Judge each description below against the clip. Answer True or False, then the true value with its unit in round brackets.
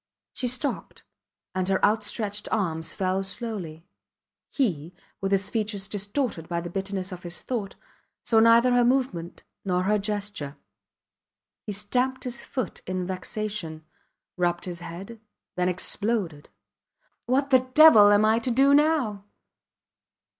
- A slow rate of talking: True (130 wpm)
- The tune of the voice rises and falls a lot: False (4.5 semitones)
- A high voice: True (205 Hz)